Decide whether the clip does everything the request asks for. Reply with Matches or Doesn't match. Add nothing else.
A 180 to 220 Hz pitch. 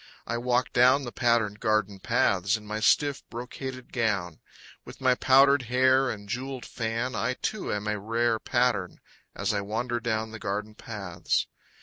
Doesn't match